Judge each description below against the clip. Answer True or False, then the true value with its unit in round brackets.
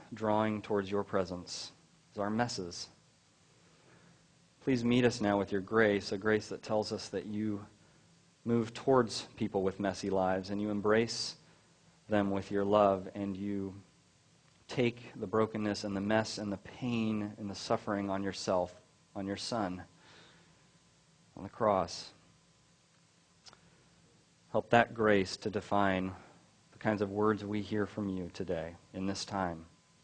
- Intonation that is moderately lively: False (2.0 semitones)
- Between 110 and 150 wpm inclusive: True (145 wpm)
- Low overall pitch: True (105 Hz)